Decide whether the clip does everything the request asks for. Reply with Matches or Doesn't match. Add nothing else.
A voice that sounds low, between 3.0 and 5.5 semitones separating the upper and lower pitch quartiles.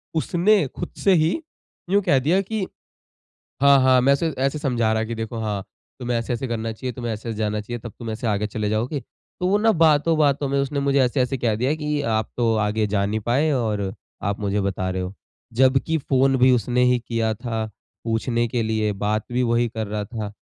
Matches